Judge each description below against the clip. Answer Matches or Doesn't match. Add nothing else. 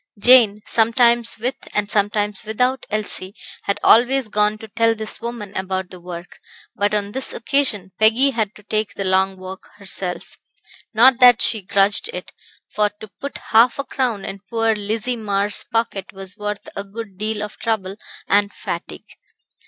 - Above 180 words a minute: Doesn't match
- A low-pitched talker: Doesn't match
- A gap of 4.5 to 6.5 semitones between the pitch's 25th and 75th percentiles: Doesn't match